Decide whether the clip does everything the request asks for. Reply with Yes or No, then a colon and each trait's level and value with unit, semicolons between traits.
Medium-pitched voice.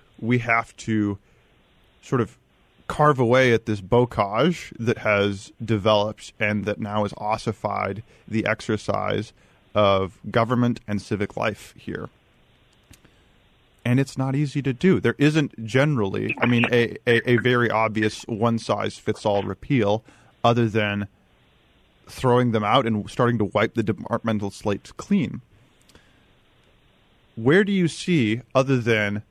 No: low, 115 Hz